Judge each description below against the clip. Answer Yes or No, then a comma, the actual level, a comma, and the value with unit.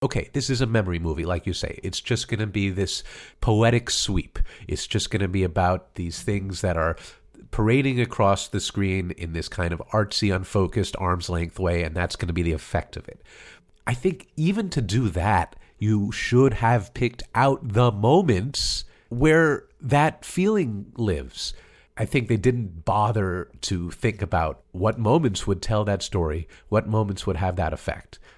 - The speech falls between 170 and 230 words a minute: Yes, average, 175 wpm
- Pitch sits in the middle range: No, low, 105 Hz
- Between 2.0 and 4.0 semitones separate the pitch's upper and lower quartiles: No, average, 4.6 semitones